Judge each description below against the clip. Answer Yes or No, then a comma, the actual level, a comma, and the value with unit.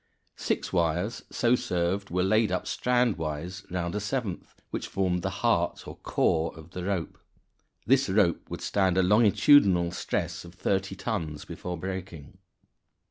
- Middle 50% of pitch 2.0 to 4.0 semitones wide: Yes, average, 3.0 semitones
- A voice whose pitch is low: Yes, very low, 95 Hz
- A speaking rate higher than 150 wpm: No, average, 145 wpm